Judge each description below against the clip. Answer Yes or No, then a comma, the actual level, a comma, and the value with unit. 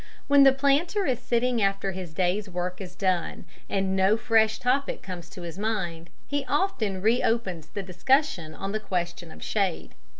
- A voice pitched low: No, high, 195 Hz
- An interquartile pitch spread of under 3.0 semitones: No, wide, 5.4 semitones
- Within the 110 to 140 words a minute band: No, average, 175 wpm